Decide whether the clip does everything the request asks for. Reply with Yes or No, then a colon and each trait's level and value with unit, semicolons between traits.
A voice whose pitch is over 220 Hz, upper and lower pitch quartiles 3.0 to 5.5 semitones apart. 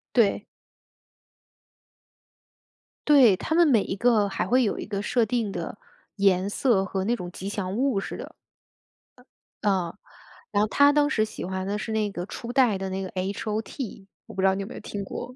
No: high, 205 Hz; average, 3.8 semitones